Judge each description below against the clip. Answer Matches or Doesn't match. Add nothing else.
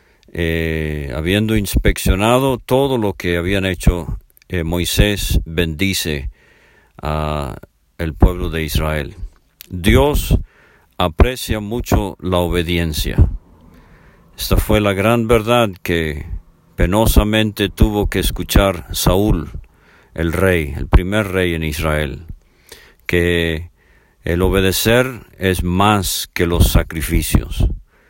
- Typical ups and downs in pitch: Matches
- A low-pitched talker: Matches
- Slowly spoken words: Matches